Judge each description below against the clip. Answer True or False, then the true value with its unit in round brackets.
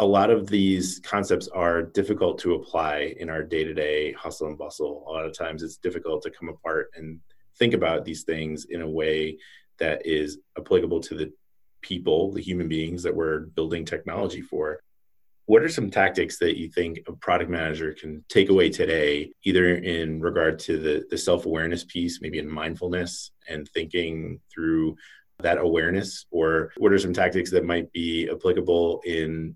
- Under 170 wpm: False (175 wpm)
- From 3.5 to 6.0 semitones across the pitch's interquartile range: False (2.5 semitones)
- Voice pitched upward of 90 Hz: False (85 Hz)